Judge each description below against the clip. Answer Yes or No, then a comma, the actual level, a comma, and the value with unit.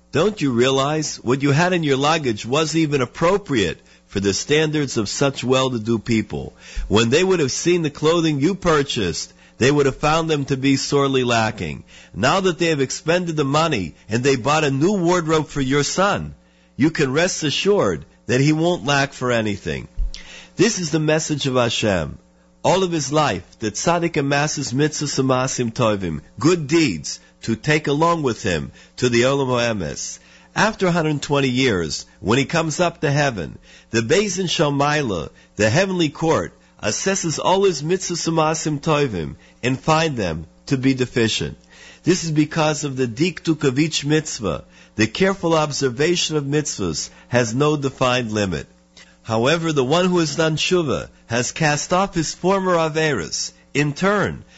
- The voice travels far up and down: Yes, wide, 5.7 semitones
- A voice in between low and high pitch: Yes, medium, 145 Hz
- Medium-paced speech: Yes, average, 160 wpm